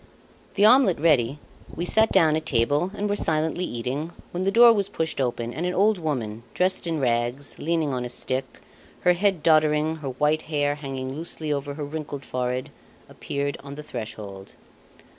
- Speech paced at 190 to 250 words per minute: No, average, 180 wpm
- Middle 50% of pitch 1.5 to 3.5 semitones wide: No, average, 4.4 semitones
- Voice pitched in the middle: Yes, medium, 150 Hz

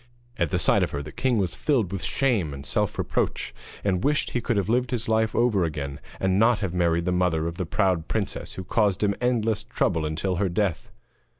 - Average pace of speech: No, fast, 220 wpm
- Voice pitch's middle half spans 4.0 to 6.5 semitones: Yes, average, 4.7 semitones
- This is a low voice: Yes, very low, 95 Hz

